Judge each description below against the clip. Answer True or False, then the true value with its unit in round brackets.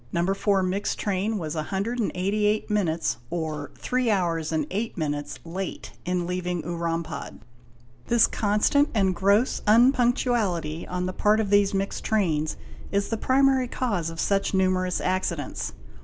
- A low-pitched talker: False (190 Hz)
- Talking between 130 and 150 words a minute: True (140 wpm)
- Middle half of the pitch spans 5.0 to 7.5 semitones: False (3.9 semitones)